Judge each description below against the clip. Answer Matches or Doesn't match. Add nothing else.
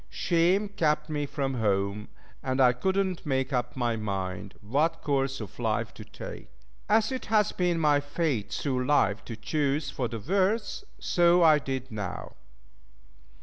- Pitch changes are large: Matches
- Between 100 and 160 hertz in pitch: Matches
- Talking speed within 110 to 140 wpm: Doesn't match